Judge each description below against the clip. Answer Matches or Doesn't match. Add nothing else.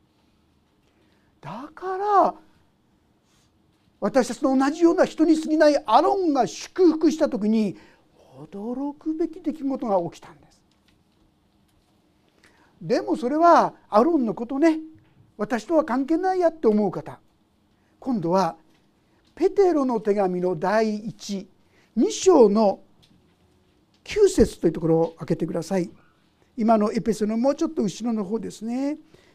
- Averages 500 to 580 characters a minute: Doesn't match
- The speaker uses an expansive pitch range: Matches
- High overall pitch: Matches